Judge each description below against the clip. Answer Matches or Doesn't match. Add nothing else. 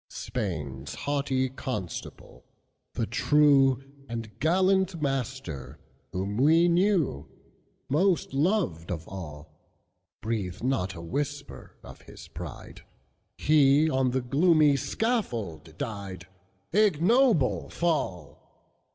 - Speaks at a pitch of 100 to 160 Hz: Matches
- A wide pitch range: Matches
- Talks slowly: Matches